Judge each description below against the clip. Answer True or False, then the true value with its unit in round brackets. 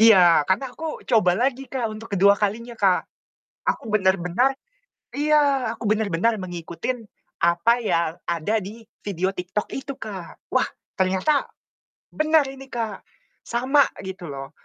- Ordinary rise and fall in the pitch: False (5.8 semitones)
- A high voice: True (215 Hz)